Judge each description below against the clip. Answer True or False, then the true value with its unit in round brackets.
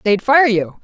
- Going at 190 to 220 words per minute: True (215 wpm)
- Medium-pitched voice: False (220 Hz)